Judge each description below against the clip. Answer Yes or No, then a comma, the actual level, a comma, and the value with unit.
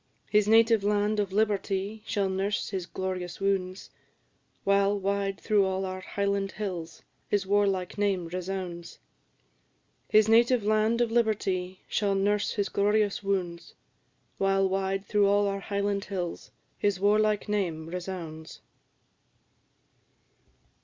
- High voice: Yes, high, 200 Hz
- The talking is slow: Yes, slow, 120 wpm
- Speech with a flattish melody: Yes, narrow, 1.6 semitones